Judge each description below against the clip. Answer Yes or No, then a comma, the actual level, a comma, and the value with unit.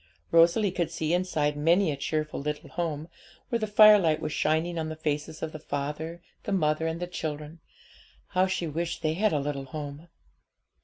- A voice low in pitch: No, medium, 160 Hz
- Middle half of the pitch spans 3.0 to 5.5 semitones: No, narrow, 2.5 semitones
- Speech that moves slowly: No, average, 185 wpm